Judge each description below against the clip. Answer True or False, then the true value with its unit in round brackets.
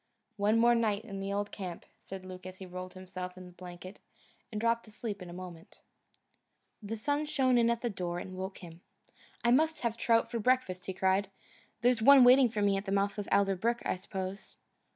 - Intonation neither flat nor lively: True (4.0 semitones)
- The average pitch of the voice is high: True (200 Hz)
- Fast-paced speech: True (215 wpm)